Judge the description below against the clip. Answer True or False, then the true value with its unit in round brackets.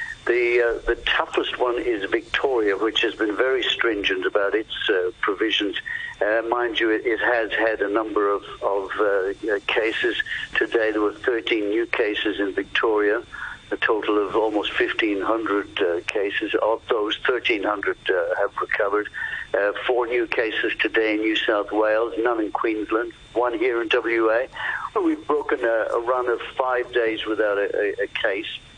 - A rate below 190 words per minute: True (165 wpm)